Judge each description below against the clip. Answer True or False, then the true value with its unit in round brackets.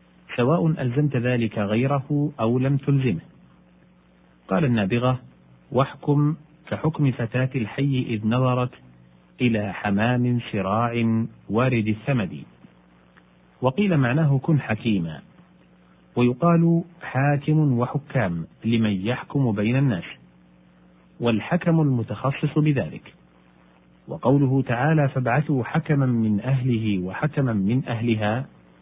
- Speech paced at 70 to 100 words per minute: True (90 wpm)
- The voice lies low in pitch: True (120 Hz)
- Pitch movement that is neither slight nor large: False (6.5 semitones)